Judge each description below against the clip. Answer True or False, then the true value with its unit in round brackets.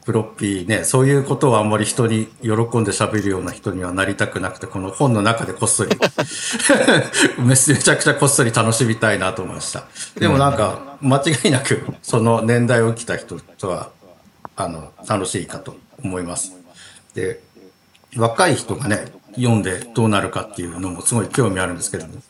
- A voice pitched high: False (115 Hz)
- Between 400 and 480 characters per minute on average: False (355 characters per minute)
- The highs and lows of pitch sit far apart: False (4.5 semitones)